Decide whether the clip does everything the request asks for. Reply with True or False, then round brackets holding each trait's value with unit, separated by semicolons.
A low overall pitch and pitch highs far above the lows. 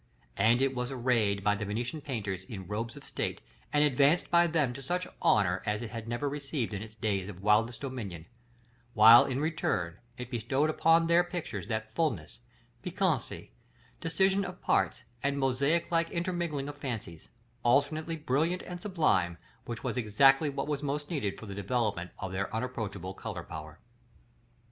True (125 Hz; 6.3 semitones)